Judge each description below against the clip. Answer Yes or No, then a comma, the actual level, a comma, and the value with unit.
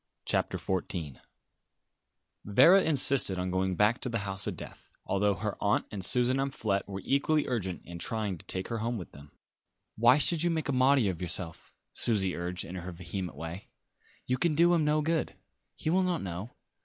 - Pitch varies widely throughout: Yes, wide, 6.9 semitones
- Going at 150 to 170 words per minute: No, average, 190 wpm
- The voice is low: Yes, low, 105 Hz